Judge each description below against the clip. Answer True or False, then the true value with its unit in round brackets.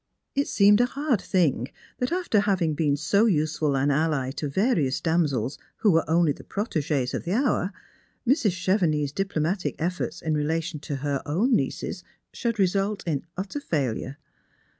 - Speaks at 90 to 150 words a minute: False (160 wpm)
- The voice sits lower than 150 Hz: False (165 Hz)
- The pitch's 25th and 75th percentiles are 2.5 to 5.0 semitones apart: False (5.5 semitones)